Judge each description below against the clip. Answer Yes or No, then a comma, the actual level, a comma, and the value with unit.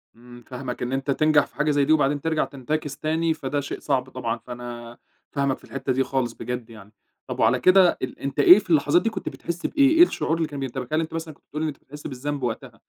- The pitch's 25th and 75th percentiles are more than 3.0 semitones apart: Yes, average, 3.8 semitones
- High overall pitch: No, medium, 140 Hz